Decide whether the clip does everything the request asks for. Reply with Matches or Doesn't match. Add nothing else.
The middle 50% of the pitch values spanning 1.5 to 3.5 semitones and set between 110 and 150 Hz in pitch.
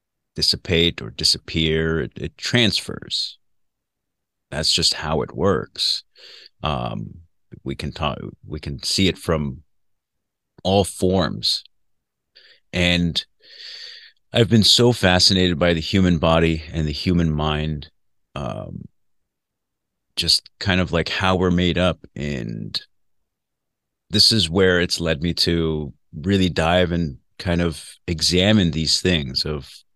Doesn't match